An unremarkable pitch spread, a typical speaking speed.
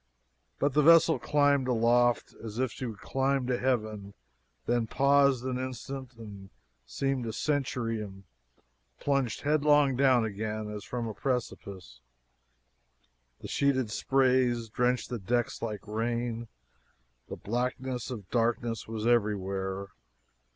No: average, 3.3 semitones; slow, 125 wpm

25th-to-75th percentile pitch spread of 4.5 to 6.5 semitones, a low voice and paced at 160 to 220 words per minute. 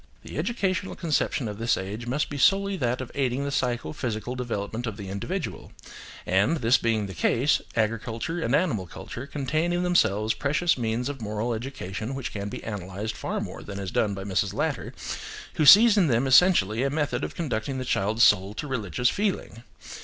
Yes: wide, 5.4 semitones; low, 120 Hz; average, 190 wpm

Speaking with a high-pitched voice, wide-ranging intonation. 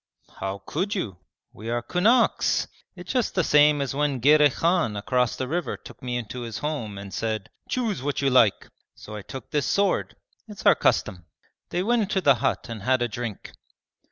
No: low, 135 Hz; wide, 7.6 semitones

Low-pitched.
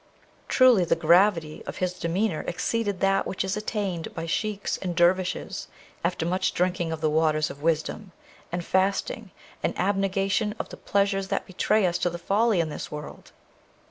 No: medium, 185 Hz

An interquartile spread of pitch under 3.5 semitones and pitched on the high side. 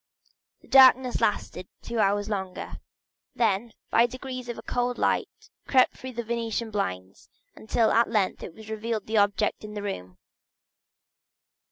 Yes: average, 2.8 semitones; high, 220 Hz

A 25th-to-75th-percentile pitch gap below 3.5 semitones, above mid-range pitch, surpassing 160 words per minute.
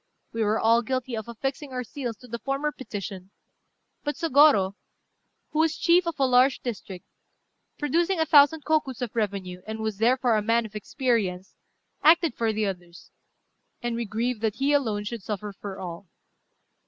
No: average, 4.8 semitones; high, 235 Hz; average, 170 wpm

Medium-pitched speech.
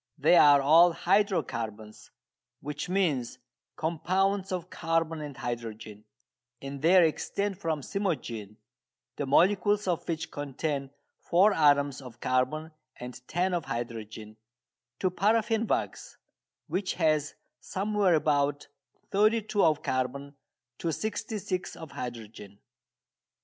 Yes: medium, 155 Hz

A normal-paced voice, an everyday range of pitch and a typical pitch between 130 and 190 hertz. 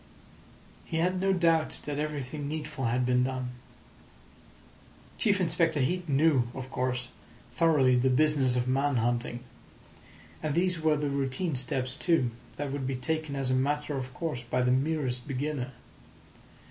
Yes: average, 150 wpm; average, 3.5 semitones; medium, 140 Hz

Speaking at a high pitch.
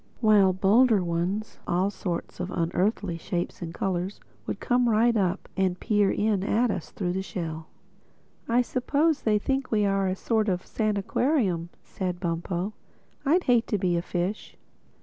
Yes: high, 195 Hz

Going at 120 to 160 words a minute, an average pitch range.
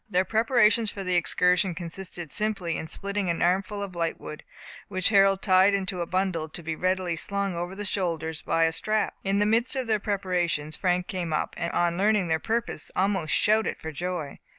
No: average, 195 wpm; average, 3.0 semitones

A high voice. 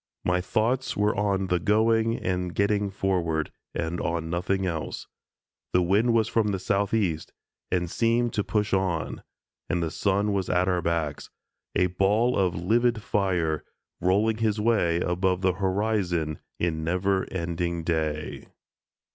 No: very low, 95 Hz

